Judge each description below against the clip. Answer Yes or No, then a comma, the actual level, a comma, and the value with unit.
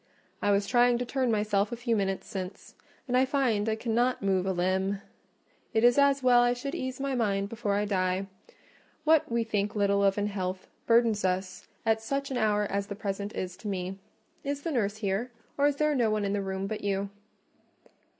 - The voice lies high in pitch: Yes, high, 210 Hz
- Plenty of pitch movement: No, average, 3.7 semitones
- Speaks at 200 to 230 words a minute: Yes, fast, 205 wpm